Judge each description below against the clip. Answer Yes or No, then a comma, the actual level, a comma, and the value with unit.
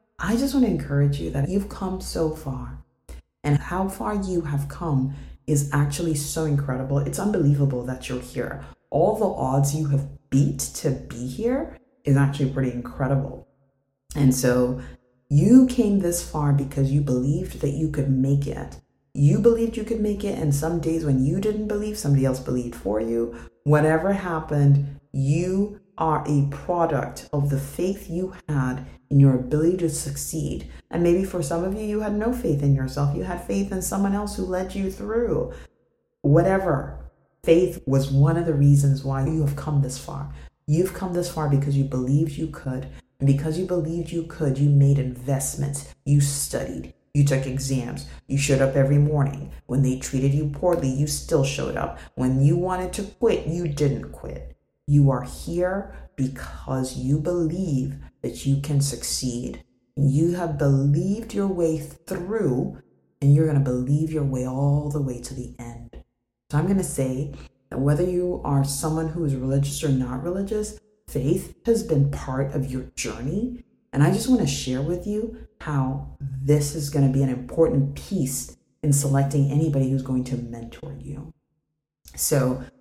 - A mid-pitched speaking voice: Yes, medium, 145 Hz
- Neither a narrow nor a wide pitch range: Yes, average, 3.9 semitones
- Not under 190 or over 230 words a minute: No, average, 180 wpm